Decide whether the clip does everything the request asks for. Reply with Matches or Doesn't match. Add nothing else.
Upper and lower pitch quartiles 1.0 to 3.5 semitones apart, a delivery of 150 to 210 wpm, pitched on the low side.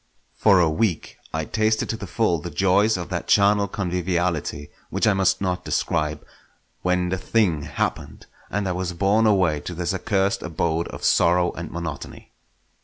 Matches